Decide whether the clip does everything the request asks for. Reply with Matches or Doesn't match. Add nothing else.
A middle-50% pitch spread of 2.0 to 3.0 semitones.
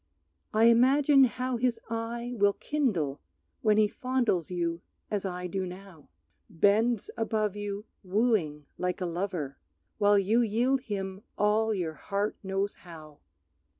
Doesn't match